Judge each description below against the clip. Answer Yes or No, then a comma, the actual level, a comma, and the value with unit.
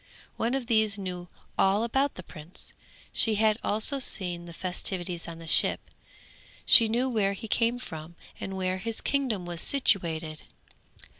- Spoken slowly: No, average, 155 wpm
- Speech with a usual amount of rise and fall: Yes, average, 4.6 semitones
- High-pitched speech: Yes, high, 195 Hz